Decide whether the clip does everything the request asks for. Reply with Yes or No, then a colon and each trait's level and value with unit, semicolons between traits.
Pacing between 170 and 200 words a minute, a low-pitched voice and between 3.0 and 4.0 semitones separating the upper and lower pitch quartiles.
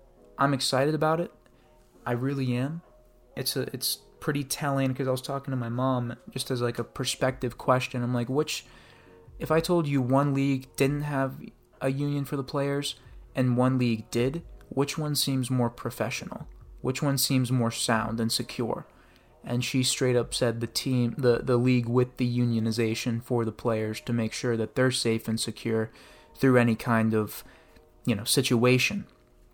No: average, 180 wpm; low, 125 Hz; narrow, 2.6 semitones